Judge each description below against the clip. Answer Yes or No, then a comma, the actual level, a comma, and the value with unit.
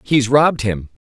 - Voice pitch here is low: Yes, low, 125 Hz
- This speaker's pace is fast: No, average, 160 wpm